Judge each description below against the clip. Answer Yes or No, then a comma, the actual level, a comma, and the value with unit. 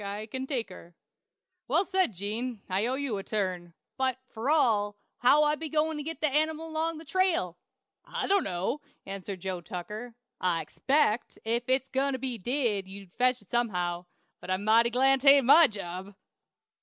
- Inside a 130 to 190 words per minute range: Yes, average, 180 wpm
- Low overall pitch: No, high, 240 Hz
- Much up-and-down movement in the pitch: Yes, wide, 6.3 semitones